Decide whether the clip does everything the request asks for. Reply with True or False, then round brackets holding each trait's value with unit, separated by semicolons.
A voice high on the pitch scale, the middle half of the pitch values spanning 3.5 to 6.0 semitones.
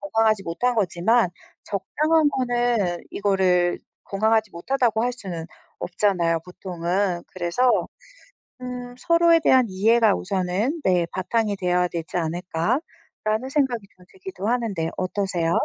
True (200 Hz; 5.4 semitones)